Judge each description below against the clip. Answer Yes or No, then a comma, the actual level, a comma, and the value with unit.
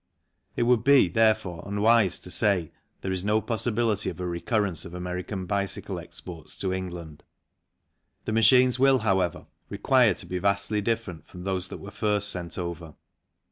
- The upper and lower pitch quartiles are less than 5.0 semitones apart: Yes, average, 3.6 semitones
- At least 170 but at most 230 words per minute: No, average, 160 wpm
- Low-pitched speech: Yes, low, 100 Hz